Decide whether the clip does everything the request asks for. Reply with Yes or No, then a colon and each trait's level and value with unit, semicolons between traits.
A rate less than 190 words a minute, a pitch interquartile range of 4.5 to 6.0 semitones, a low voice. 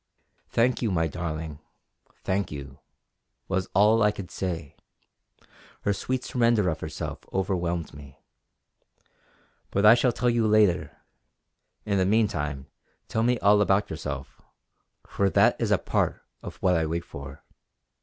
Yes: average, 140 wpm; average, 5.1 semitones; very low, 95 Hz